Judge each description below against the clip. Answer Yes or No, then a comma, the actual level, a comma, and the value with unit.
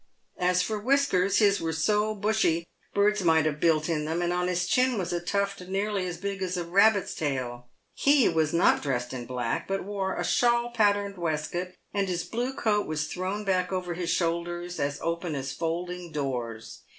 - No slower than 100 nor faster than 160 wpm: No, average, 190 wpm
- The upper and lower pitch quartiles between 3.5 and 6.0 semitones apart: Yes, average, 3.8 semitones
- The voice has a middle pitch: Yes, medium, 180 Hz